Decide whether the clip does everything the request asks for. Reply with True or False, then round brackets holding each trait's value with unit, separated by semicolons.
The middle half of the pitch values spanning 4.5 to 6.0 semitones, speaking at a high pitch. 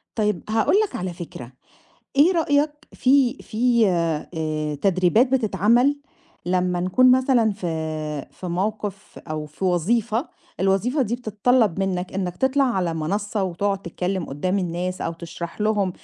True (5.2 semitones; 195 Hz)